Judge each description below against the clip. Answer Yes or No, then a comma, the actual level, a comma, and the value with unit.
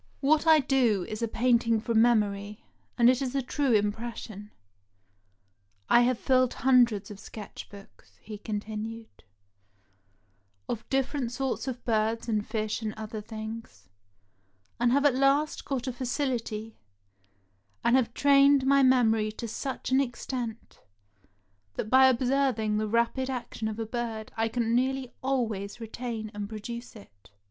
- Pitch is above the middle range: Yes, high, 235 Hz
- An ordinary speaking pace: Yes, average, 145 wpm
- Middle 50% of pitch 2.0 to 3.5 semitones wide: Yes, average, 3.1 semitones